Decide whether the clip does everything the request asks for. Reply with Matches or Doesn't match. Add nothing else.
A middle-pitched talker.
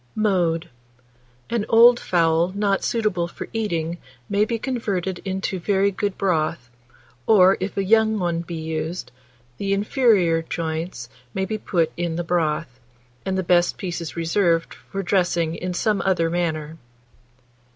Matches